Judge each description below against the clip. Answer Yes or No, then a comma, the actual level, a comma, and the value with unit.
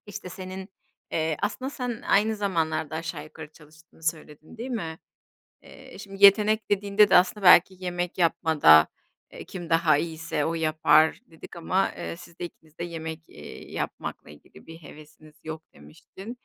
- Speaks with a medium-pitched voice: Yes, medium, 165 Hz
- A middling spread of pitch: Yes, average, 3.5 semitones